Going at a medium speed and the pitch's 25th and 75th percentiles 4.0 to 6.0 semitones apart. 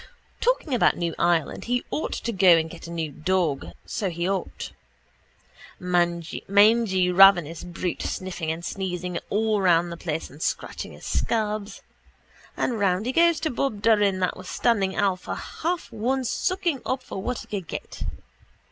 Yes: average, 165 wpm; average, 4.8 semitones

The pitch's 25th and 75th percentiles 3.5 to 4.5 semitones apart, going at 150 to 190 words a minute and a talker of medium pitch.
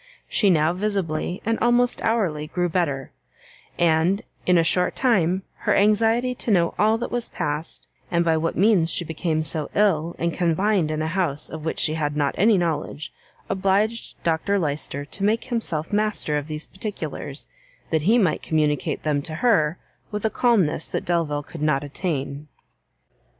No: average, 5.1 semitones; average, 170 wpm; medium, 170 Hz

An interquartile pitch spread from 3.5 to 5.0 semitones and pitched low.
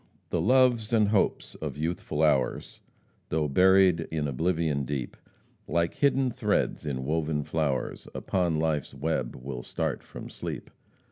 Yes: average, 4.3 semitones; very low, 80 Hz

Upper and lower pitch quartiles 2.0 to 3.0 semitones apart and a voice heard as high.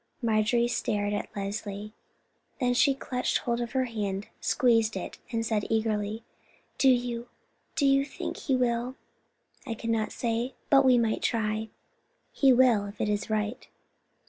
Yes: narrow, 2.6 semitones; high, 230 Hz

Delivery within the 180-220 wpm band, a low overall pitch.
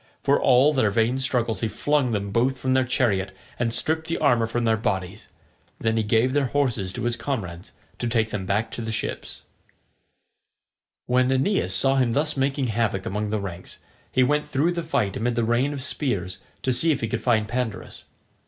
Yes: average, 200 wpm; low, 120 Hz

